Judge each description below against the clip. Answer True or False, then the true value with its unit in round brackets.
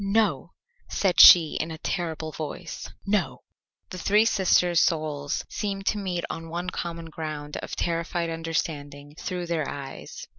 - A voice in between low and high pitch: True (165 Hz)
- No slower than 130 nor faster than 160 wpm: True (145 wpm)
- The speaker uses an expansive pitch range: False (2.7 semitones)